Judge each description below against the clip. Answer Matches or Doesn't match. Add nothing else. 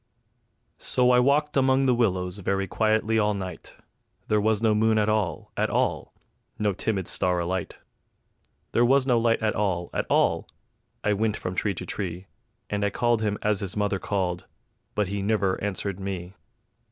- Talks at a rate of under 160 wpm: Doesn't match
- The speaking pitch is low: Matches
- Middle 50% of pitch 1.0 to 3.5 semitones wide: Matches